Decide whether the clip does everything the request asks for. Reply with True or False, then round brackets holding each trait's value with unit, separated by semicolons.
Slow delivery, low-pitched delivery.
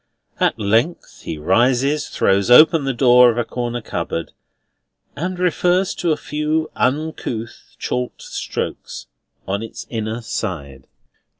True (125 wpm; 125 Hz)